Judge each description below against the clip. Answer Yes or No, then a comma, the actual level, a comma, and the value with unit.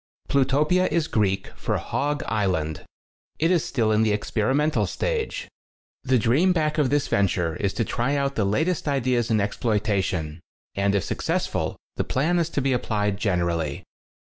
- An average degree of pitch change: No, wide, 6.7 semitones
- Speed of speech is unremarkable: Yes, average, 165 wpm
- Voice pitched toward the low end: Yes, low, 120 Hz